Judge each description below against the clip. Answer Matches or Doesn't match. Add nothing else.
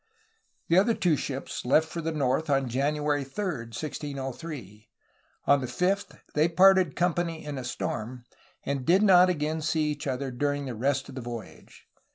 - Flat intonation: Doesn't match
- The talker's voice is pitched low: Doesn't match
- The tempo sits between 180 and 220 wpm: Doesn't match